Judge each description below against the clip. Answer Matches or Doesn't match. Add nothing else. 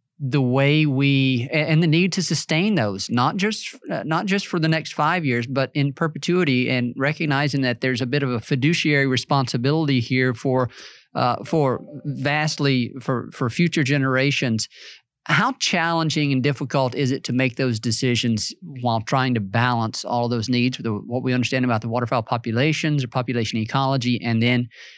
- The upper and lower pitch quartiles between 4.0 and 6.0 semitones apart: Doesn't match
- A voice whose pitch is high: Doesn't match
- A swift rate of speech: Doesn't match